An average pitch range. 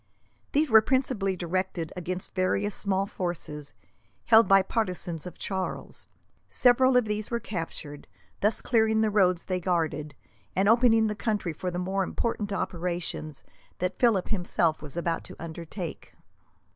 Yes: average, 4.0 semitones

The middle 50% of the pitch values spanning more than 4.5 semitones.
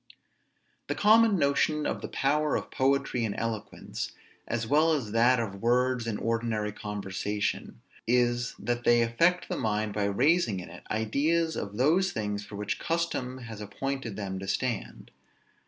Yes: average, 4.9 semitones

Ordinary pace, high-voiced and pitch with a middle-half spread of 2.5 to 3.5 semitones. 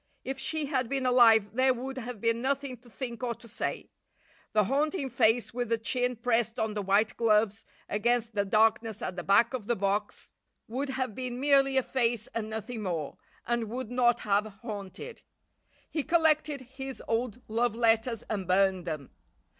Yes: average, 180 wpm; high, 235 Hz; average, 3.2 semitones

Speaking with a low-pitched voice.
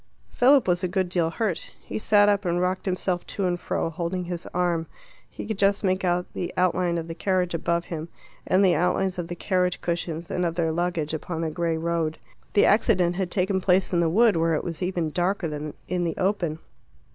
No: medium, 175 Hz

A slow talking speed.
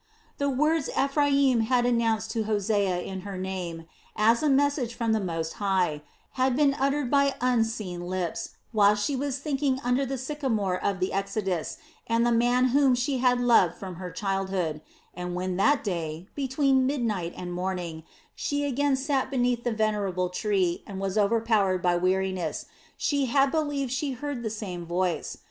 No: average, 165 wpm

